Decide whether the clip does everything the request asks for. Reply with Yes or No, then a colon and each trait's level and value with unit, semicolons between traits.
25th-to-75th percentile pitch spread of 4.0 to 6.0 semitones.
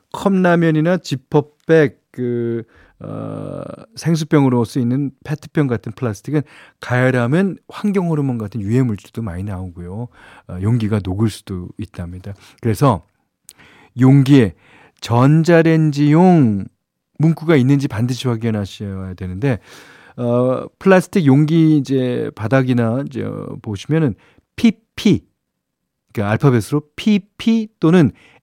Yes: wide, 5.5 semitones